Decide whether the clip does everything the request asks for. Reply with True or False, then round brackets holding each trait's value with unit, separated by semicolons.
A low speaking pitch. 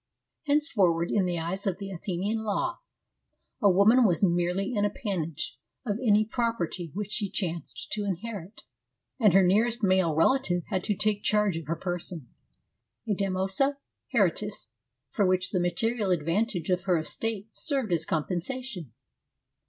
False (195 Hz)